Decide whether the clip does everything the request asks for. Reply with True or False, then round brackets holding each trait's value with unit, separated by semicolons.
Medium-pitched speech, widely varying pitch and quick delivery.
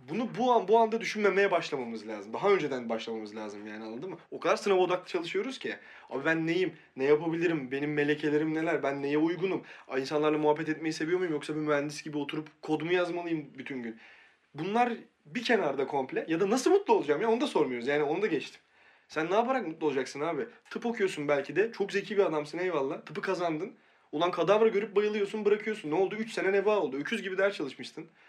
True (170 Hz; 5.8 semitones; 205 wpm)